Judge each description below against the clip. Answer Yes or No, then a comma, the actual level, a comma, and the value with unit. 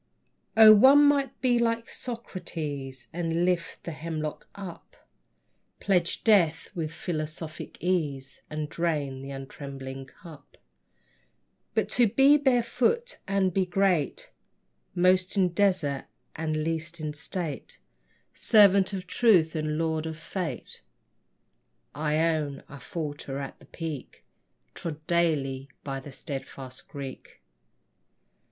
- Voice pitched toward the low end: No, medium, 165 Hz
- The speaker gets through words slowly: Yes, slow, 115 wpm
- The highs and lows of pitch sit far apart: No, average, 4.6 semitones